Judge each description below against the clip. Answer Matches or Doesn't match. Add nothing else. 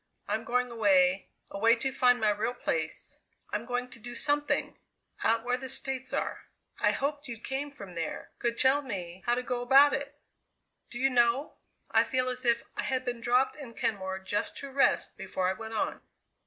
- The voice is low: Doesn't match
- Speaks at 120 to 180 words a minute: Doesn't match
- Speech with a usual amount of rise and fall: Matches